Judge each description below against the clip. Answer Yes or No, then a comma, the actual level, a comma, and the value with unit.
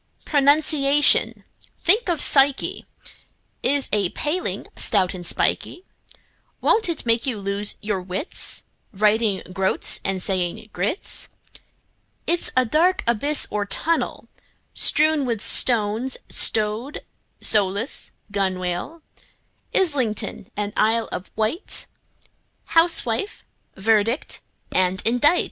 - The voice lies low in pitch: No, high, 225 Hz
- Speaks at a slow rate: Yes, slow, 100 wpm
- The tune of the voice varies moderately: No, wide, 6.5 semitones